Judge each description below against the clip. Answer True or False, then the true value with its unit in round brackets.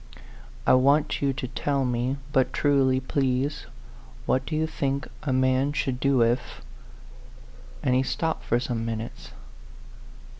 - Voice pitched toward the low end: True (130 Hz)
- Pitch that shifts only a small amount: True (1.9 semitones)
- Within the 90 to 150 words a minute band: True (145 wpm)